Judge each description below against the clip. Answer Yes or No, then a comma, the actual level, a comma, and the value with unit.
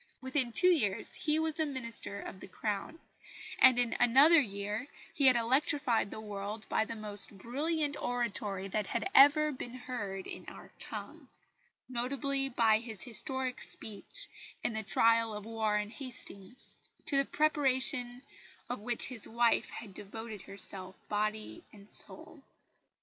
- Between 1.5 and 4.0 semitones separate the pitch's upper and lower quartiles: No, average, 4.4 semitones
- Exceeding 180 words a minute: No, average, 145 wpm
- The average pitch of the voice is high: Yes, high, 235 Hz